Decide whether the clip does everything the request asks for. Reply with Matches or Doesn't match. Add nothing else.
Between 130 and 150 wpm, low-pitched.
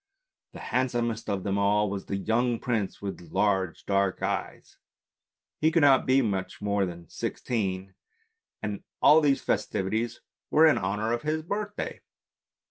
Matches